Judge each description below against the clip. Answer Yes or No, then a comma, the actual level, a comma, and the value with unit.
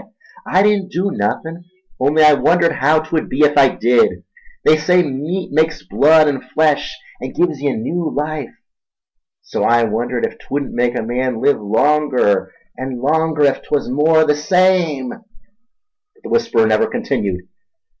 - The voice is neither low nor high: Yes, medium, 150 Hz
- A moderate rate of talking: Yes, average, 155 wpm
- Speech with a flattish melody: No, average, 4.0 semitones